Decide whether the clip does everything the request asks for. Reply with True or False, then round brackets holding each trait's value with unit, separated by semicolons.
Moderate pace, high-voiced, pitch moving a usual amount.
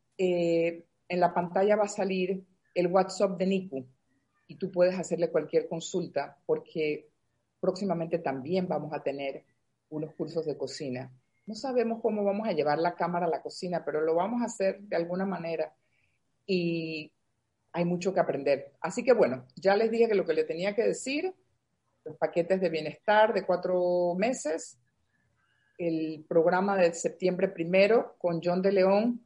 False (165 wpm; 175 Hz; 3.7 semitones)